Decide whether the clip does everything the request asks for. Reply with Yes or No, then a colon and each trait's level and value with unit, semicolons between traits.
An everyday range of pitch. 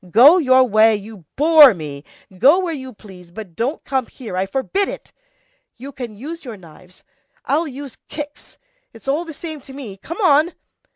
No: wide, 6.1 semitones